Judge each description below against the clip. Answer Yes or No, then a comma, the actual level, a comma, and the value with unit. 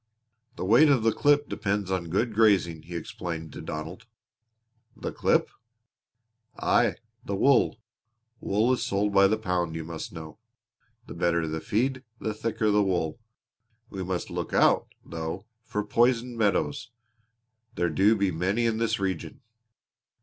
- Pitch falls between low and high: No, low, 100 Hz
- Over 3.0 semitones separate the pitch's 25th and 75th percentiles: Yes, average, 4.7 semitones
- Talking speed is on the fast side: No, average, 150 wpm